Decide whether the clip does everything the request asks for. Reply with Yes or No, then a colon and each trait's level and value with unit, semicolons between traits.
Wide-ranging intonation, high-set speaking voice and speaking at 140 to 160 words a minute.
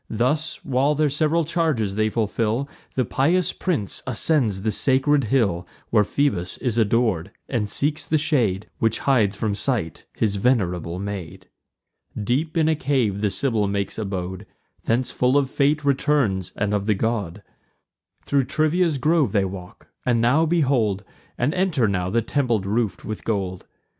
No: wide, 5.9 semitones; low, 115 Hz; average, 155 wpm